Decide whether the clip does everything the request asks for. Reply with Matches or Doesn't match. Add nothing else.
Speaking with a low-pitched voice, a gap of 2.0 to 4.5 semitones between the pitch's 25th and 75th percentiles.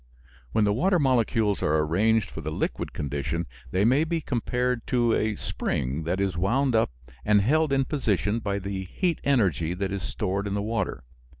Doesn't match